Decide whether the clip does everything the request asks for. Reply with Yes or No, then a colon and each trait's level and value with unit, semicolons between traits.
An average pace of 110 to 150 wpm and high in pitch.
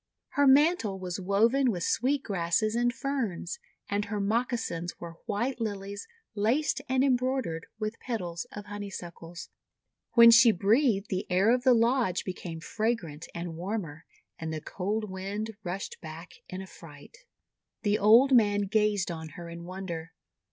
Yes: average, 145 wpm; high, 205 Hz